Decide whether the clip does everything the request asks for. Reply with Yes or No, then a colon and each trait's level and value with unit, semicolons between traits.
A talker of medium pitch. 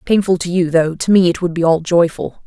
Yes: medium, 175 Hz